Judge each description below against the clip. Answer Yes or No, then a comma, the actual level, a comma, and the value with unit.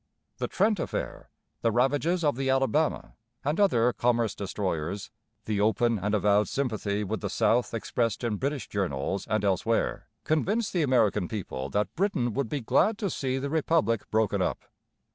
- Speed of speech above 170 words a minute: No, average, 160 wpm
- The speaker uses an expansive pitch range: Yes, wide, 5.8 semitones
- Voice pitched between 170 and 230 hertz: No, low, 120 Hz